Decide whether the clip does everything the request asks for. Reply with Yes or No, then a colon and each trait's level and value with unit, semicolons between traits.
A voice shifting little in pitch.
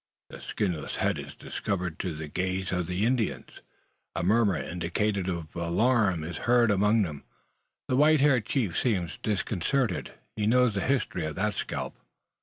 No: average, 5.0 semitones